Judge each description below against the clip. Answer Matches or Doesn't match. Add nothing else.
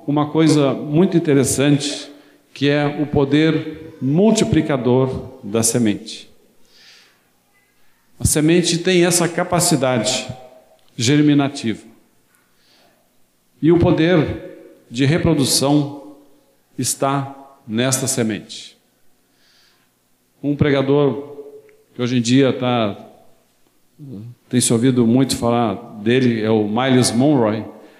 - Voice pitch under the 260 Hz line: Matches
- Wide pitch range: Doesn't match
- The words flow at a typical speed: Doesn't match